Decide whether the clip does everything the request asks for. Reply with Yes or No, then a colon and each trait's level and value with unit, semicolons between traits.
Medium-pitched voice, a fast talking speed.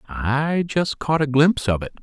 Yes: medium, 145 Hz; fast, 210 wpm